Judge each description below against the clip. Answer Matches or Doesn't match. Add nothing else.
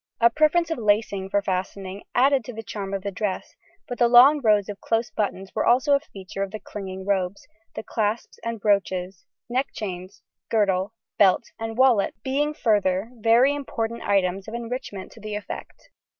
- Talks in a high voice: Matches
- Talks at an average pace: Matches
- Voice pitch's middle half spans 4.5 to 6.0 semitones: Doesn't match